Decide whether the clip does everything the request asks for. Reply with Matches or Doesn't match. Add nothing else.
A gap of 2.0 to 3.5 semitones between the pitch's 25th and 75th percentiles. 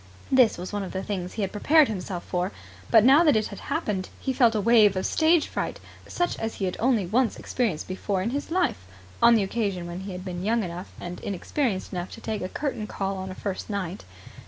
Doesn't match